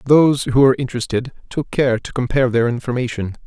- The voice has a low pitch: Yes, low, 125 Hz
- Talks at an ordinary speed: Yes, average, 175 wpm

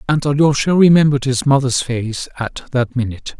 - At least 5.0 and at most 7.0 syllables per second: Yes, 5.5 syllables/s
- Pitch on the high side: No, low, 130 Hz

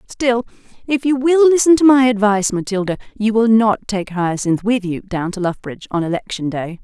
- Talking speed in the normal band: Yes, average, 195 wpm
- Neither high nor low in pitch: No, high, 215 Hz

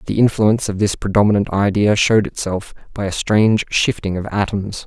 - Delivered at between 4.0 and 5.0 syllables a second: No, 5.6 syllables/s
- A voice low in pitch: Yes, low, 105 Hz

